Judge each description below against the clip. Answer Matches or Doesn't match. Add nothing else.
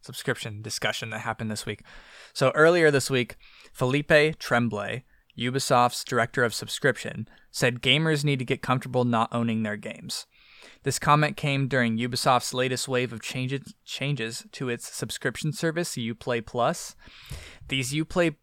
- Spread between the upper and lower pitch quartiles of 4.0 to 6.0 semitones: Doesn't match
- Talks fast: Doesn't match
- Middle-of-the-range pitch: Doesn't match